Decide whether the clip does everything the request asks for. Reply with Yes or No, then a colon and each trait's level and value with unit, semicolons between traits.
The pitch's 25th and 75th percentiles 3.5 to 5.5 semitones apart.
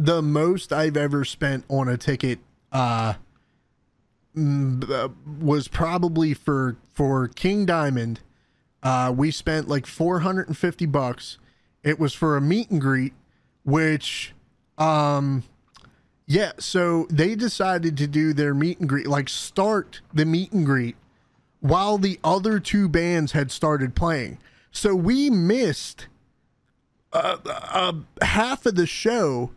Yes: average, 4.5 semitones